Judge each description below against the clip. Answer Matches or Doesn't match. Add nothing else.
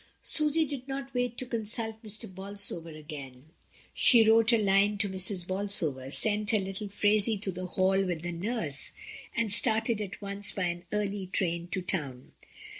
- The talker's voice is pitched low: Doesn't match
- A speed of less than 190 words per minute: Matches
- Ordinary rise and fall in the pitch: Matches